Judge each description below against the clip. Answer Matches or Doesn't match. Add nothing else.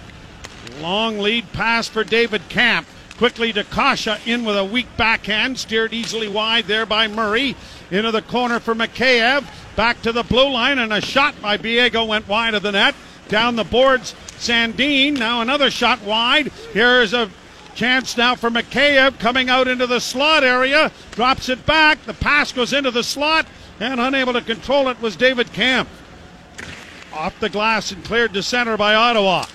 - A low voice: Doesn't match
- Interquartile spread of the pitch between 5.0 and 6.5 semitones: Doesn't match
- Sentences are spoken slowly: Doesn't match